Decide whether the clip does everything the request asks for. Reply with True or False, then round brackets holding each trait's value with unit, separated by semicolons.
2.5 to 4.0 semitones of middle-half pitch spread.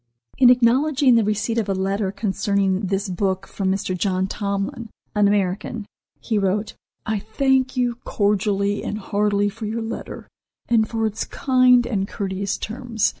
True (2.9 semitones)